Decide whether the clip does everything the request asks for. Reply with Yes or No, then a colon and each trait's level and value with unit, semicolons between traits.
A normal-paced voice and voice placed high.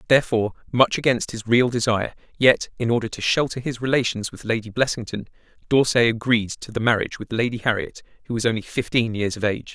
No: average, 190 wpm; low, 115 Hz